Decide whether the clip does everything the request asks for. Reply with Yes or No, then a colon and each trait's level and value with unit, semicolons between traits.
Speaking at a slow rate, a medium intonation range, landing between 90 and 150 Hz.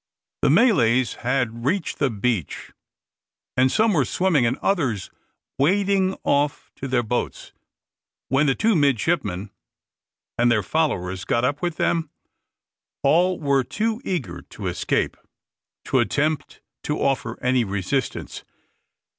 No: slow, 125 wpm; wide, 6.0 semitones; medium, 140 Hz